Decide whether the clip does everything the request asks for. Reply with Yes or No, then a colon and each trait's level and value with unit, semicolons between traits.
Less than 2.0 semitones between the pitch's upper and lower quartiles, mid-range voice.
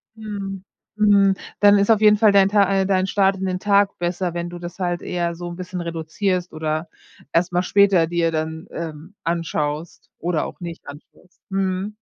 No: average, 2.7 semitones; medium, 180 Hz